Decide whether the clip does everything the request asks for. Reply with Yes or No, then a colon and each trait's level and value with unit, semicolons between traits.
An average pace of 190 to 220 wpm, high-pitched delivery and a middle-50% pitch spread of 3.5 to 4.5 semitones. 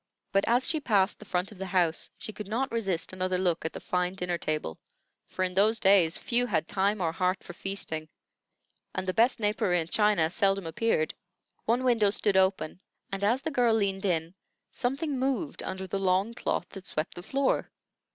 Yes: average, 195 wpm; high, 195 Hz; average, 3.8 semitones